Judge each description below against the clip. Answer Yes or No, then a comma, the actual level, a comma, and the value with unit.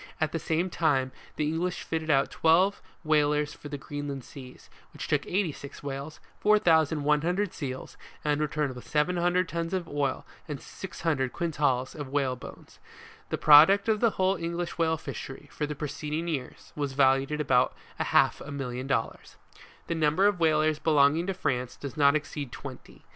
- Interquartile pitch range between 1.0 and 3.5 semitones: Yes, average, 3.1 semitones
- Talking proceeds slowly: No, average, 170 wpm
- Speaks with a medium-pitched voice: Yes, medium, 150 Hz